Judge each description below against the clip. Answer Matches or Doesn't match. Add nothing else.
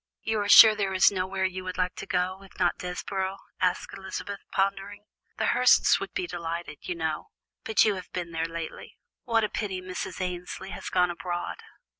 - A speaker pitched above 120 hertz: Matches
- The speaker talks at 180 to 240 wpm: Matches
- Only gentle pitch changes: Matches